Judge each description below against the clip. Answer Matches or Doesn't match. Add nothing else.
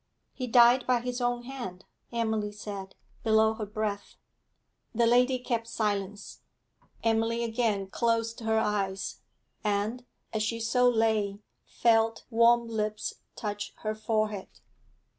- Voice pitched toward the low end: Doesn't match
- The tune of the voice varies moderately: Doesn't match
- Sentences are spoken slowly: Matches